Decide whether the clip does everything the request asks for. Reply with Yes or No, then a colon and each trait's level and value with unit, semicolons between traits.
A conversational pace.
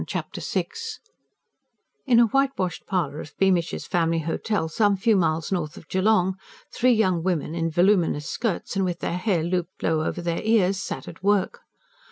Yes: average, 170 wpm